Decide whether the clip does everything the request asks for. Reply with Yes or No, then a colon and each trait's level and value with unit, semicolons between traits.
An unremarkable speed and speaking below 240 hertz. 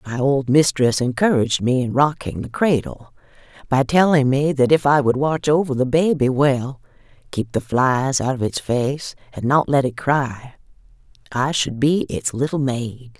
Yes: average, 175 wpm; low, 135 Hz